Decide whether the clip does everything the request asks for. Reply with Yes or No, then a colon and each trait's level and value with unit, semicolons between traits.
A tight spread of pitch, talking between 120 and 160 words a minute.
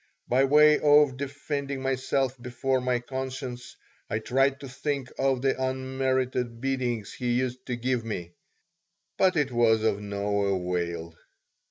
Yes: narrow, 2.3 semitones; average, 140 wpm